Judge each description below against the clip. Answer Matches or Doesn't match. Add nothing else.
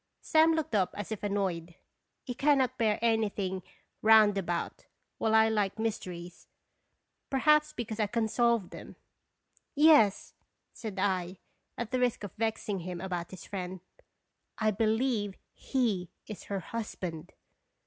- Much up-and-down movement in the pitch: Doesn't match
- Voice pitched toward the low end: Doesn't match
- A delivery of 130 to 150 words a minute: Matches